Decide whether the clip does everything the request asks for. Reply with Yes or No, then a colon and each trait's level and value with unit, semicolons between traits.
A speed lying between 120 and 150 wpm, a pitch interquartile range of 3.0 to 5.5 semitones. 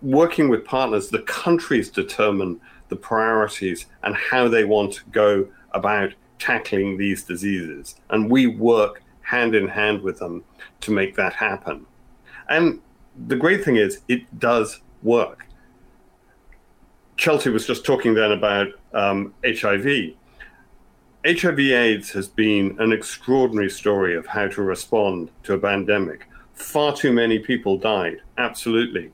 Yes: slow, 135 wpm; average, 3.5 semitones